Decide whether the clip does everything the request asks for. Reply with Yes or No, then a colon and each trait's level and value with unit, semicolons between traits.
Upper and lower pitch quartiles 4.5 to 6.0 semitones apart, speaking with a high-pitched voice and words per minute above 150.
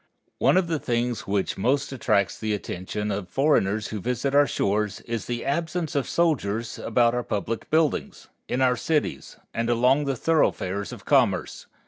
No: average, 5.1 semitones; low, 120 Hz; average, 165 wpm